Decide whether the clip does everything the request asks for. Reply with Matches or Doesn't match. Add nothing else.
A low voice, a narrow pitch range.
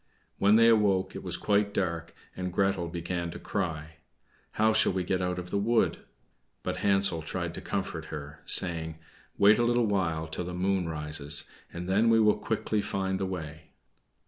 Doesn't match